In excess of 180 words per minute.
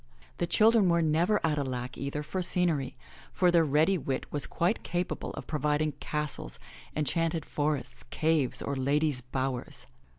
No: average, 155 wpm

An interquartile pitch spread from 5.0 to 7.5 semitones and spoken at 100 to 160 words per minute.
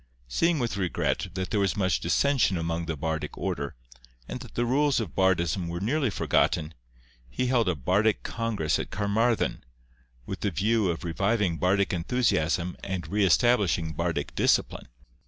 Yes: average, 5.3 semitones; average, 155 wpm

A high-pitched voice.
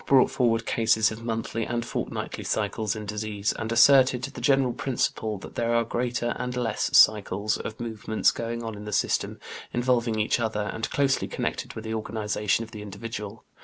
No: low, 115 Hz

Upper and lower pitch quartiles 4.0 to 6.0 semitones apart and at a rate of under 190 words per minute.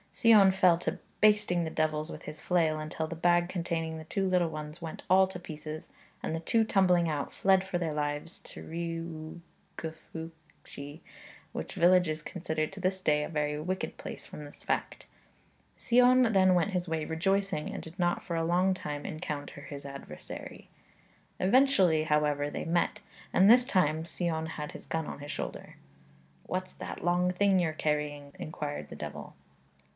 No: average, 3.2 semitones; average, 170 wpm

